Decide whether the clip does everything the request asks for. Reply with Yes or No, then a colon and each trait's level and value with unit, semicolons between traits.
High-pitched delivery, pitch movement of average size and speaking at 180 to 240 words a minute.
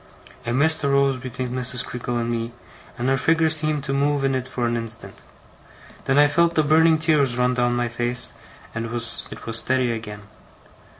No: low, 130 Hz; average, 3.4 semitones; average, 185 wpm